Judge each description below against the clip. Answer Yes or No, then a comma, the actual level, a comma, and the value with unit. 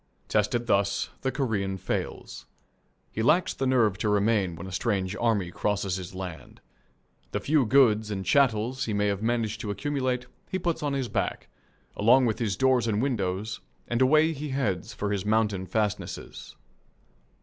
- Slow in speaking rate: No, average, 165 wpm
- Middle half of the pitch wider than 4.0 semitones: Yes, average, 4.5 semitones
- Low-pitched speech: Yes, low, 110 Hz